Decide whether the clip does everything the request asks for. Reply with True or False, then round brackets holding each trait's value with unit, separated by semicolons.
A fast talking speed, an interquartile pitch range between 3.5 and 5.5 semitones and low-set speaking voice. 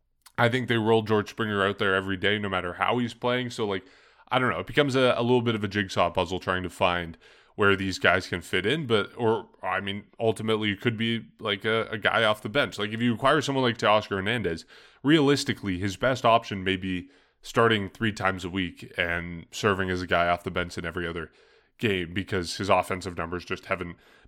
True (225 wpm; 4.0 semitones; 100 Hz)